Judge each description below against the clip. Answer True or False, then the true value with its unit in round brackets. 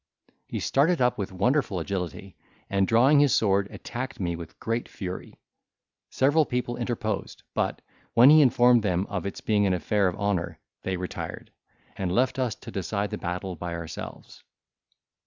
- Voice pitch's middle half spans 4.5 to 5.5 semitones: True (5.1 semitones)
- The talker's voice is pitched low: True (100 Hz)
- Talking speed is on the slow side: False (160 wpm)